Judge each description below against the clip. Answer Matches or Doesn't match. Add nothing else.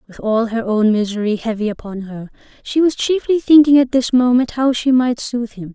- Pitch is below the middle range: Doesn't match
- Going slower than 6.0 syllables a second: Matches